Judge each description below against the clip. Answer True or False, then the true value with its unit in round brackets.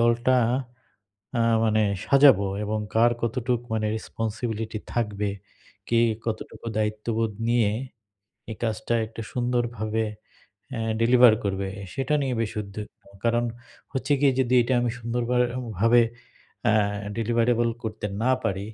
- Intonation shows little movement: True (1.9 semitones)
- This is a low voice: True (115 Hz)